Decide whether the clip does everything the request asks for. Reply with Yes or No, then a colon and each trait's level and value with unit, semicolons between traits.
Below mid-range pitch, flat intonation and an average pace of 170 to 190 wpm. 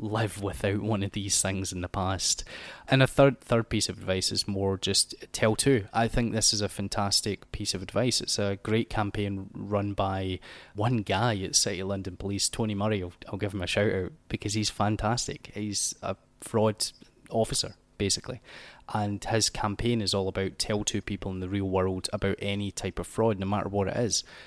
No: low, 100 Hz; narrow, 2.2 semitones; fast, 205 wpm